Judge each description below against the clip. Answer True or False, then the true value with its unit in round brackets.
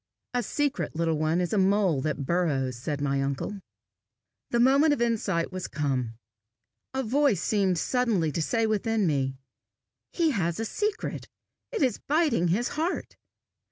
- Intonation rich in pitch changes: True (7.9 semitones)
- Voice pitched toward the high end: True (195 Hz)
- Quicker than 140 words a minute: True (155 wpm)